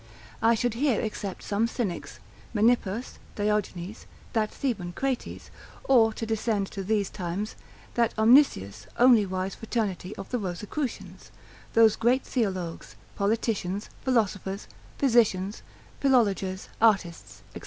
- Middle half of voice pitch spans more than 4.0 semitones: No, average, 3.5 semitones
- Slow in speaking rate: Yes, slow, 115 wpm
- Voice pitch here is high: Yes, high, 215 Hz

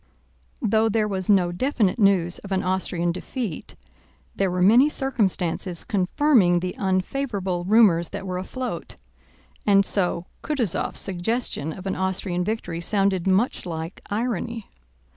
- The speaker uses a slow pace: Yes, slow, 130 wpm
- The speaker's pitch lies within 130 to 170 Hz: No, high, 190 Hz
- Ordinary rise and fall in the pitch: Yes, average, 3.6 semitones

